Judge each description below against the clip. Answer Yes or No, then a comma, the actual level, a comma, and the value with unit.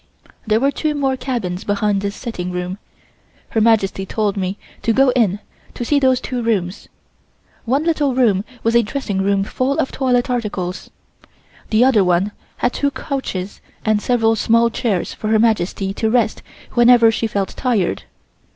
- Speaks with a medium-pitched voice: No, high, 225 Hz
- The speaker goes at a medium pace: Yes, average, 165 wpm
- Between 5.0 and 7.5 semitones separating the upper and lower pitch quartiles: No, average, 4.0 semitones